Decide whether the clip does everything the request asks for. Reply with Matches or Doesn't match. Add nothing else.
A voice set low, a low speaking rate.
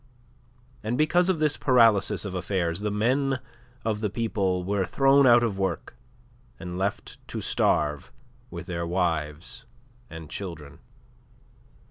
Matches